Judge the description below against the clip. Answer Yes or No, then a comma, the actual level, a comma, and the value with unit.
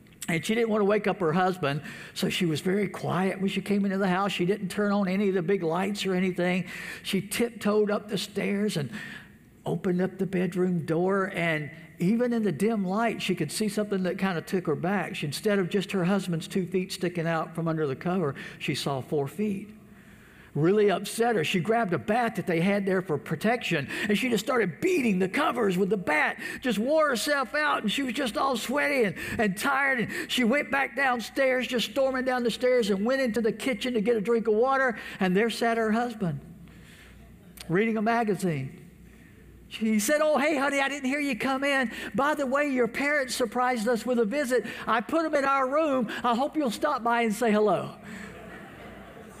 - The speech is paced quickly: Yes, fast, 215 wpm